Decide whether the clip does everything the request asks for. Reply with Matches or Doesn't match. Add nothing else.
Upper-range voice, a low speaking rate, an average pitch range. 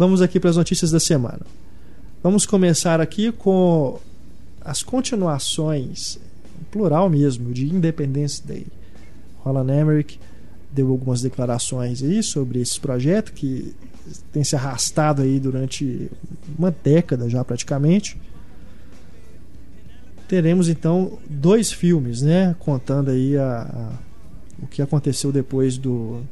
Doesn't match